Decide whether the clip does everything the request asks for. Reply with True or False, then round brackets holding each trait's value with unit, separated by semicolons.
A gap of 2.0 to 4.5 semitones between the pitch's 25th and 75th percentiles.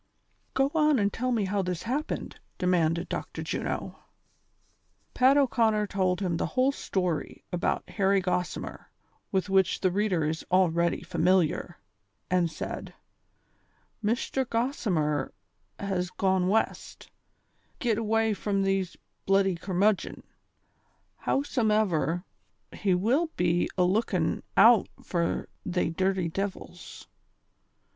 True (3.5 semitones)